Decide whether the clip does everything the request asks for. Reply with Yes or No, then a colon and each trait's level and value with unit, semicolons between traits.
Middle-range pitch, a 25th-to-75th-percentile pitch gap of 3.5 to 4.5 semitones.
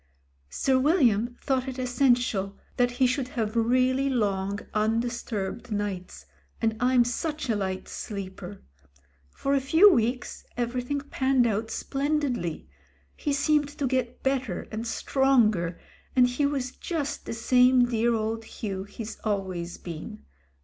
No: high, 245 Hz; average, 4.0 semitones